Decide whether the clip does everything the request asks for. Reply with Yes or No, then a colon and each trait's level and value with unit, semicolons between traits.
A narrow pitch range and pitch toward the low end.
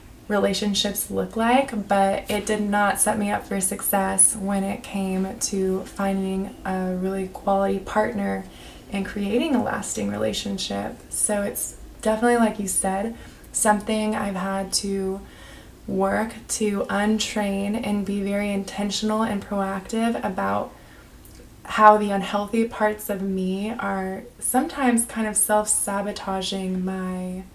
No: narrow, 1.8 semitones; high, 200 Hz